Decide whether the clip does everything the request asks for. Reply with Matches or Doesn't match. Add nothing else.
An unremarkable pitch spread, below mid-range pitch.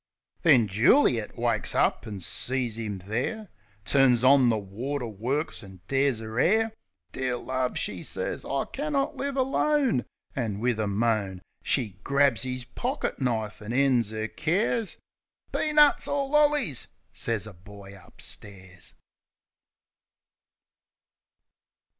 Doesn't match